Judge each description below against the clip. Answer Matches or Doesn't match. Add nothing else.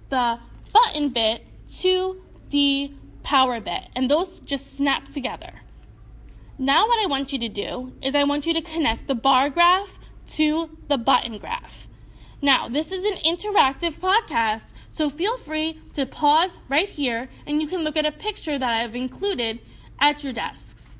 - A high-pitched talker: Matches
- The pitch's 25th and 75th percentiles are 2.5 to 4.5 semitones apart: Matches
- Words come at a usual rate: Matches